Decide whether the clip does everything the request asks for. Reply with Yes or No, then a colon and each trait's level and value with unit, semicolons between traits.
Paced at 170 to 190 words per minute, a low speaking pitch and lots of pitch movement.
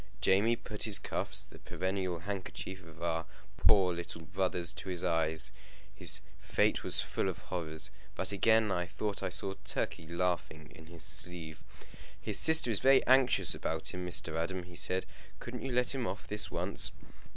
No: average, 175 wpm; very low, 90 Hz; average, 3.7 semitones